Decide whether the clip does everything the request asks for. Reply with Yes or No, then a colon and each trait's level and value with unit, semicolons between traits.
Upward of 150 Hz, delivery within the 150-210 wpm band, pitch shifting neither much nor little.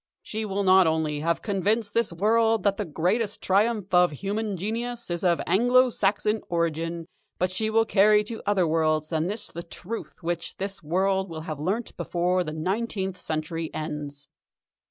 Yes: high, 190 Hz; average, 170 wpm; average, 4.3 semitones